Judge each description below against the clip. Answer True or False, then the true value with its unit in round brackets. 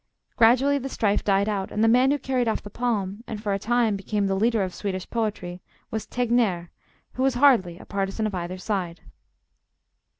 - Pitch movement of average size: True (3.8 semitones)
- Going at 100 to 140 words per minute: False (195 wpm)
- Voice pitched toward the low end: False (210 Hz)